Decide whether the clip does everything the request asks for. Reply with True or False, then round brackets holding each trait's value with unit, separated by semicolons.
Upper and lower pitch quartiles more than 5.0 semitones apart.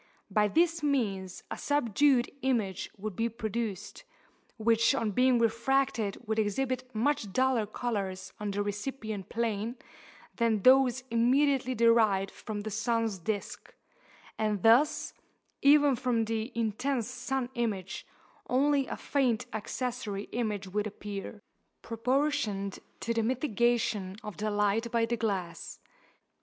False (3.5 semitones)